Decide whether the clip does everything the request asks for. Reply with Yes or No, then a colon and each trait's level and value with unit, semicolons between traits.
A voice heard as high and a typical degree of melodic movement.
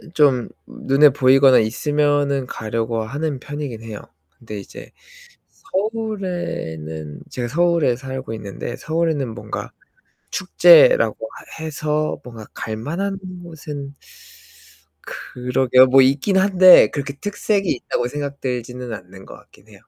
No: medium, 140 Hz; average, 4.8 semitones